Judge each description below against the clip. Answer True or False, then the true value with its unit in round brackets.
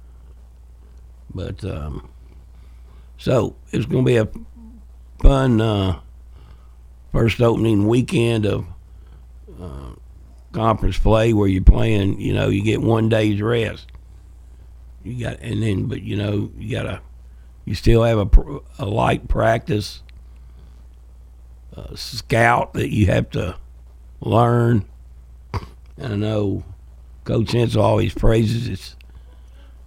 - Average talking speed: False (120 wpm)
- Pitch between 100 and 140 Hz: False (85 Hz)